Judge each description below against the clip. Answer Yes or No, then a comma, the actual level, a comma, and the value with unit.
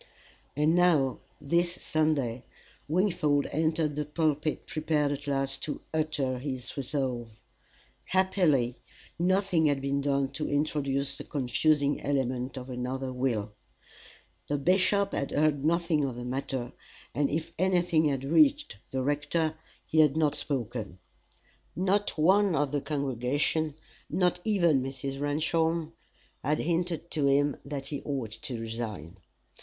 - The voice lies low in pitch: No, medium, 145 Hz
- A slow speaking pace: Yes, slow, 130 wpm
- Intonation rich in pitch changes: No, average, 3.2 semitones